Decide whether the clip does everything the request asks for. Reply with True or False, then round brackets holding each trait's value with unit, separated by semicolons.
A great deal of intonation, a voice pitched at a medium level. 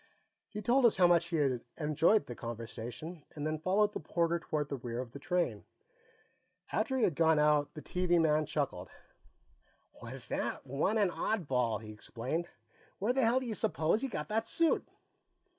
True (6.3 semitones; 160 Hz)